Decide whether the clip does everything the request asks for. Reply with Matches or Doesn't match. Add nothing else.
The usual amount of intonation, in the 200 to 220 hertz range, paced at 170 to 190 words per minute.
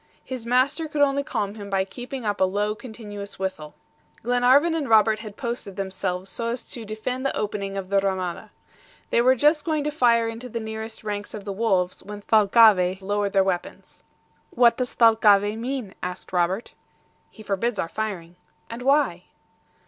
Matches